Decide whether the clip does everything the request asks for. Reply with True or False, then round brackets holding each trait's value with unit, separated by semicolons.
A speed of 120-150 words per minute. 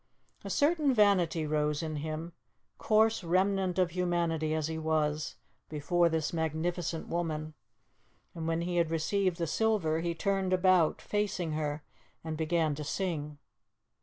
True (140 wpm)